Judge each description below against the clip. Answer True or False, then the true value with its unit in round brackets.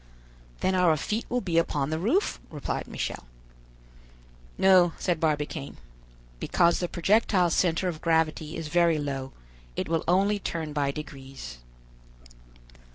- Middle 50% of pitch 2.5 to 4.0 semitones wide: True (3.2 semitones)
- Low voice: False (165 Hz)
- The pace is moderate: False (130 wpm)